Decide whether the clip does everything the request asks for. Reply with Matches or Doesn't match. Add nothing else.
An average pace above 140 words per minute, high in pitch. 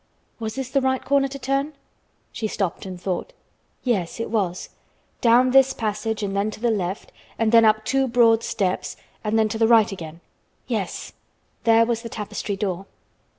Matches